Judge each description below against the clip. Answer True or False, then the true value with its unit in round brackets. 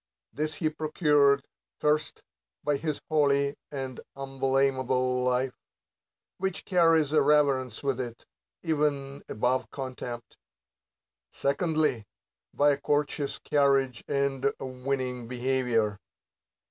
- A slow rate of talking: True (100 wpm)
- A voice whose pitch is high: False (140 Hz)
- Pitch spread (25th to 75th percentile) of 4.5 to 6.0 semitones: False (2.5 semitones)